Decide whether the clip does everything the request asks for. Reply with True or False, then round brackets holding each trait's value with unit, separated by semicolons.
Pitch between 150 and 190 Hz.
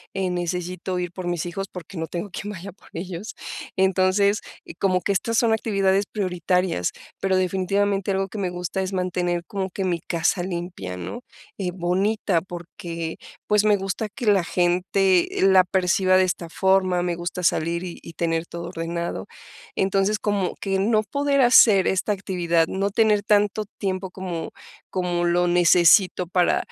True (185 Hz)